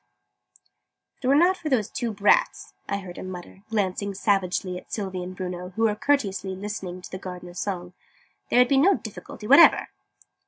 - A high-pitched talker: Yes, high, 200 Hz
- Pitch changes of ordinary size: Yes, average, 3.6 semitones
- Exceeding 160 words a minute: Yes, average, 185 wpm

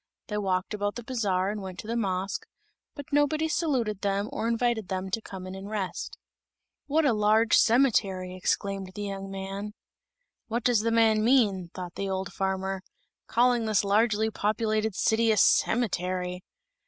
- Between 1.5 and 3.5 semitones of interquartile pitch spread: Yes, average, 3.1 semitones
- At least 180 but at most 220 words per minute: No, average, 165 wpm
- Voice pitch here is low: No, high, 210 Hz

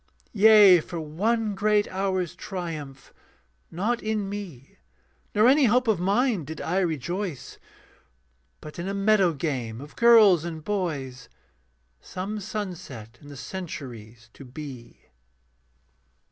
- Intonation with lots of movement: Yes, wide, 6.2 semitones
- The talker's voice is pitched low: No, medium, 180 Hz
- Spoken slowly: Yes, slow, 120 wpm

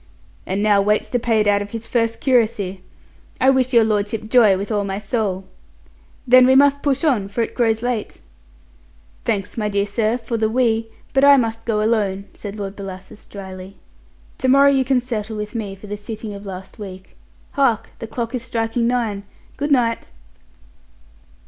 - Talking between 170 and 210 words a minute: Yes, average, 185 wpm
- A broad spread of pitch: No, average, 3.2 semitones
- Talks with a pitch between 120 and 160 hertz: No, high, 220 Hz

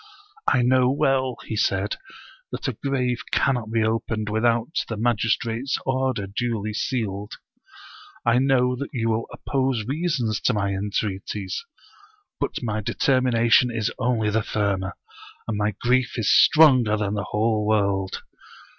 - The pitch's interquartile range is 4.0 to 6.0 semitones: No, average, 3.3 semitones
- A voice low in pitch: Yes, low, 115 Hz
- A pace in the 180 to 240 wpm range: No, average, 145 wpm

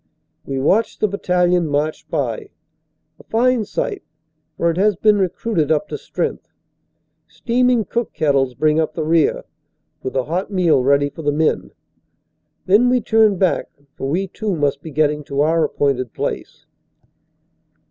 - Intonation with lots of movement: Yes, wide, 6.2 semitones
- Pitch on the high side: No, medium, 165 Hz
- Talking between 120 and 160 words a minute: Yes, average, 155 wpm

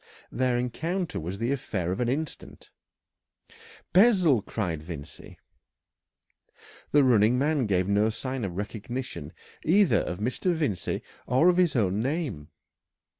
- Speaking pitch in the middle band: No, low, 120 Hz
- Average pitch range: No, wide, 7.1 semitones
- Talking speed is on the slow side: Yes, slow, 125 wpm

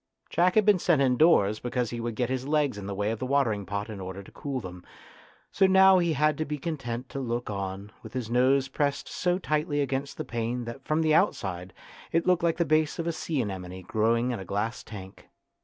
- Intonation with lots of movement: Yes, wide, 6.3 semitones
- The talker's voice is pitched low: Yes, low, 125 Hz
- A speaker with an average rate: No, fast, 230 wpm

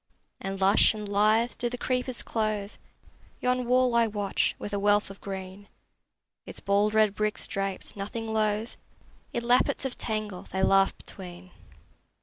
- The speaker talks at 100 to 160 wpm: Yes, average, 150 wpm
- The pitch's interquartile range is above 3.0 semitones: No, average, 2.7 semitones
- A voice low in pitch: No, high, 210 Hz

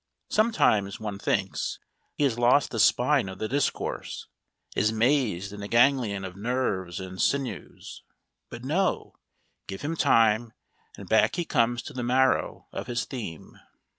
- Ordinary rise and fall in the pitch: Yes, average, 4.6 semitones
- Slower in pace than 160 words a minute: Yes, average, 150 wpm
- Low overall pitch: Yes, low, 120 Hz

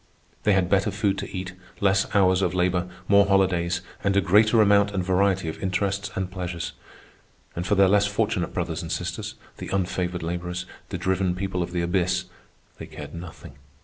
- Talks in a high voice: No, very low, 95 Hz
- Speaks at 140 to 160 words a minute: No, average, 180 wpm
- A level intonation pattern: Yes, narrow, 1.9 semitones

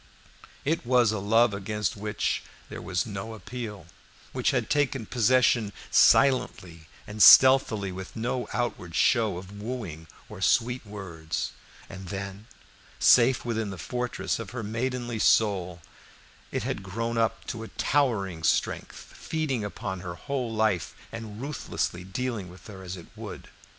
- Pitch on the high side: No, low, 110 Hz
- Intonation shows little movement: No, average, 4.2 semitones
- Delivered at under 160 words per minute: Yes, average, 145 wpm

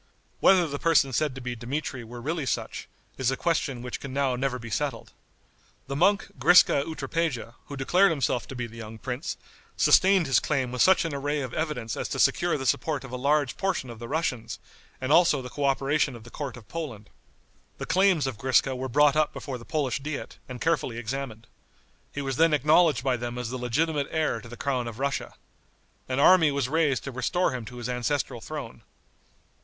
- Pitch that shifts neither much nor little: Yes, average, 3.9 semitones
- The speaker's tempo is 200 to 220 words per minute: Yes, fast, 205 wpm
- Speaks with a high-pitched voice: No, low, 135 Hz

